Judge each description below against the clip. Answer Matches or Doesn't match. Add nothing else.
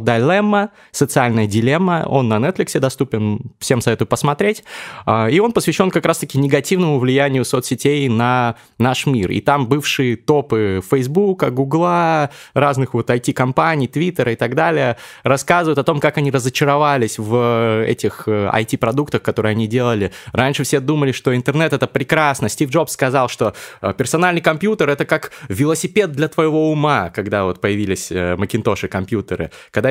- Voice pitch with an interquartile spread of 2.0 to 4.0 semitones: Doesn't match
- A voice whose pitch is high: Doesn't match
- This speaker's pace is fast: Doesn't match